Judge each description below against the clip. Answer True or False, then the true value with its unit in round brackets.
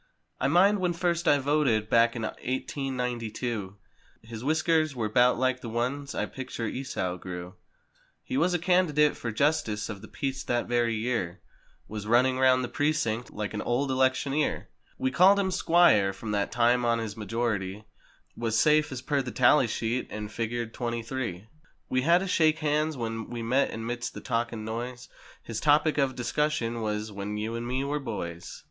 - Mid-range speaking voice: False (120 Hz)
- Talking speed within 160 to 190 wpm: True (185 wpm)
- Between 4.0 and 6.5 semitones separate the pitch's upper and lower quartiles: True (4.3 semitones)